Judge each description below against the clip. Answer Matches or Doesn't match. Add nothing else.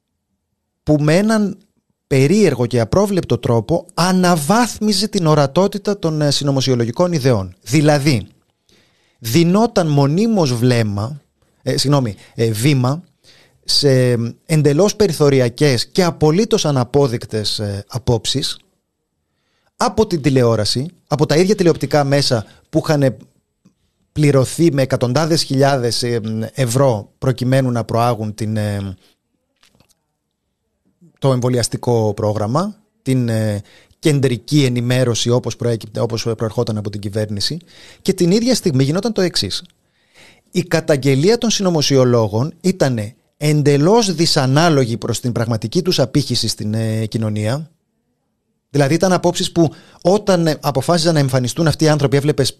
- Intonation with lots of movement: Matches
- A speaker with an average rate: Doesn't match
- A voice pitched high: Doesn't match